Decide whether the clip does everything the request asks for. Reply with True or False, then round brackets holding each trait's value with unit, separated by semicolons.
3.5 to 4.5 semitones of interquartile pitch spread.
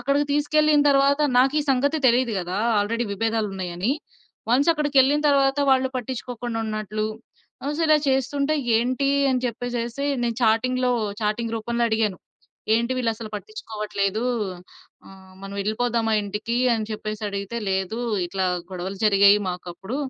True (4.1 semitones)